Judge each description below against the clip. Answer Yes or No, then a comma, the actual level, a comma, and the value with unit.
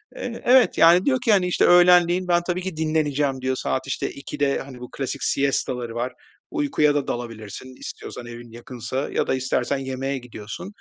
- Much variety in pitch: Yes, wide, 5.8 semitones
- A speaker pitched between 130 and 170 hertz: Yes, medium, 140 Hz